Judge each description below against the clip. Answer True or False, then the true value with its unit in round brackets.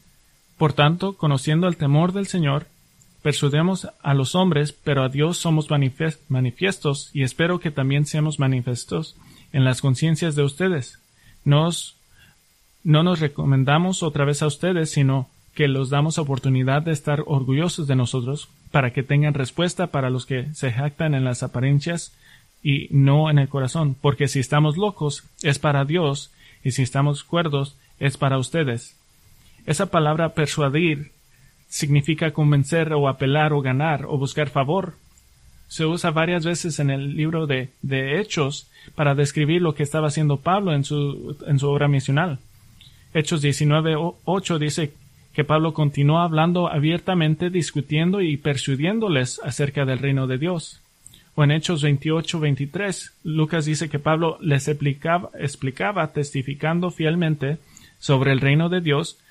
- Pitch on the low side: False (150 Hz)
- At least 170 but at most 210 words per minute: False (145 wpm)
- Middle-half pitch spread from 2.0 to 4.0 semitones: True (2.7 semitones)